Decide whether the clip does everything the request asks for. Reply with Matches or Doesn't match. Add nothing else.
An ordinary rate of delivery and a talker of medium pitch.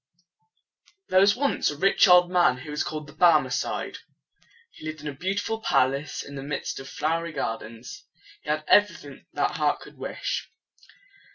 Matches